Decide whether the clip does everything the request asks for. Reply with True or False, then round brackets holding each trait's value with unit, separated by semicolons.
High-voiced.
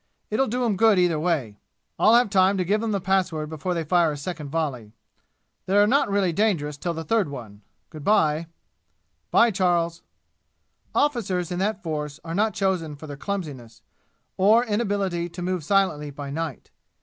False (175 Hz)